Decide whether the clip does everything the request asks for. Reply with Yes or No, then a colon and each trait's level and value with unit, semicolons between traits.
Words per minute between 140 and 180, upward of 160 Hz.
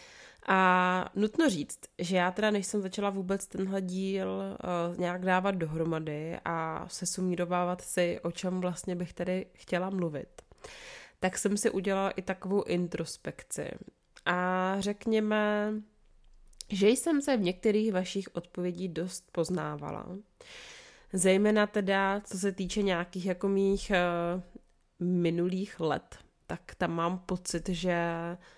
No: average, 125 wpm; medium, 185 Hz